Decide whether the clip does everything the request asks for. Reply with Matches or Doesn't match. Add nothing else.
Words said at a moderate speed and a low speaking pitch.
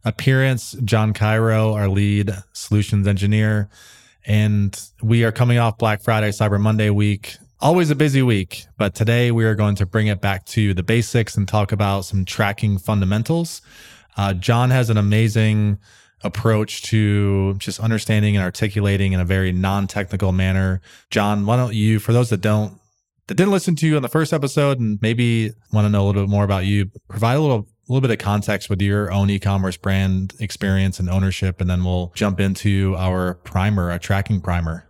Matches